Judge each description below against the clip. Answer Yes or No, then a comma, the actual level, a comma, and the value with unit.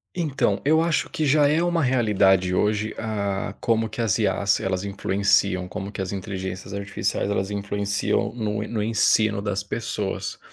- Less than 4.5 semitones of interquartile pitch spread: Yes, narrow, 2.5 semitones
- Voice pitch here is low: Yes, low, 105 Hz